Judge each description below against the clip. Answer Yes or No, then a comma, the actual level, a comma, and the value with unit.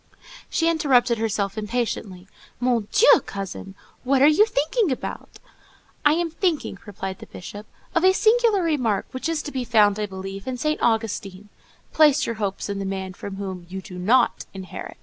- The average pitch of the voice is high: Yes, high, 225 Hz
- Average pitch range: No, wide, 7.4 semitones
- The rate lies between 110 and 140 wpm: No, average, 170 wpm